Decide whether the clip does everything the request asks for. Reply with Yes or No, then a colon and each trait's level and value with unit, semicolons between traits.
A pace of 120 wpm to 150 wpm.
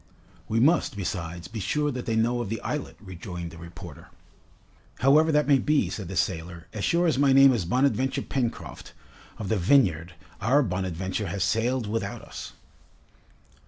No: average, 165 wpm